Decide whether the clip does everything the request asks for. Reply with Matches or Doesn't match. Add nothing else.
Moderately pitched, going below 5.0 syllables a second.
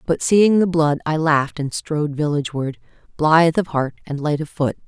Doesn't match